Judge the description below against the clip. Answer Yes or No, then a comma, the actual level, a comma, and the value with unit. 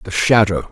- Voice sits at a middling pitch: No, low, 100 Hz